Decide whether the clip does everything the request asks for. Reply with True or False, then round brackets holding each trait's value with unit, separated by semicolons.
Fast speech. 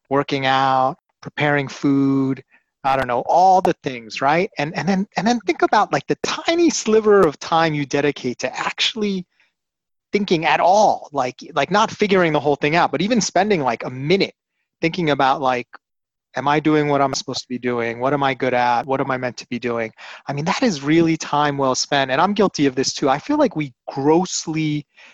True (215 wpm)